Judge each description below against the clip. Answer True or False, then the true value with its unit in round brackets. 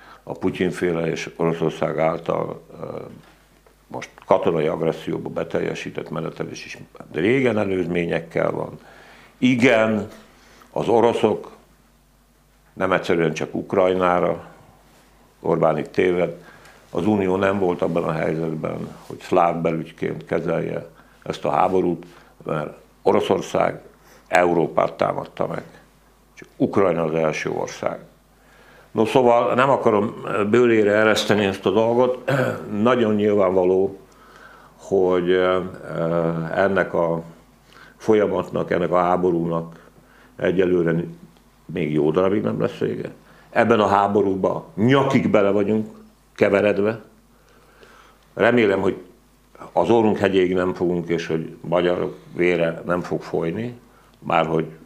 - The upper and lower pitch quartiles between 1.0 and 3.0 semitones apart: False (4.2 semitones)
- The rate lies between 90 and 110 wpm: True (105 wpm)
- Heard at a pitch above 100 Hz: False (90 Hz)